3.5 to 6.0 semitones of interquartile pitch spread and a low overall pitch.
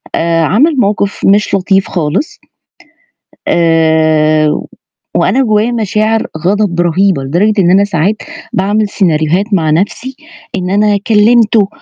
No: average, 4.2 semitones; high, 195 Hz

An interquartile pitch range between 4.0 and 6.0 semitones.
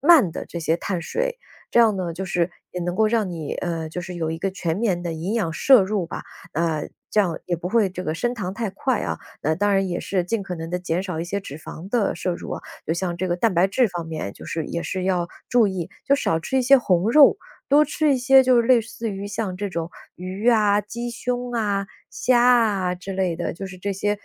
Yes: average, 4.7 semitones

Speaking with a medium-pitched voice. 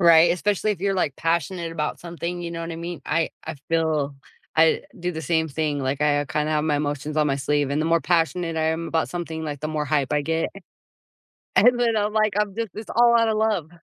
Yes: medium, 165 Hz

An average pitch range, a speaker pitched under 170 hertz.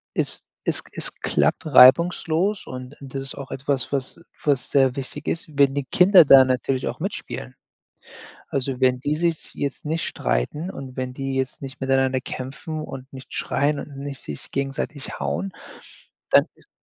No: narrow, 2.2 semitones; low, 135 Hz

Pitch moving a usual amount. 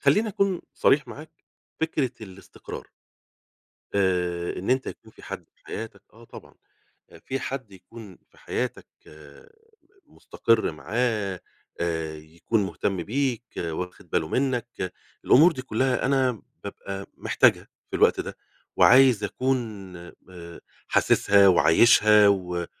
No: wide, 5.9 semitones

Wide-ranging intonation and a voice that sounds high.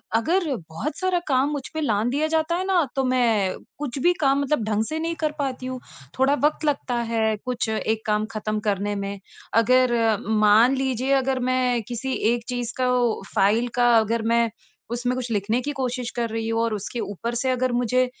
No: average, 3.3 semitones; high, 245 Hz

